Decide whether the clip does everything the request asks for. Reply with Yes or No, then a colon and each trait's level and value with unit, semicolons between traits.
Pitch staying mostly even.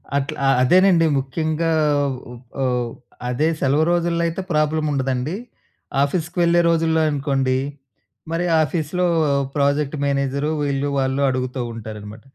No: average, 3.7 semitones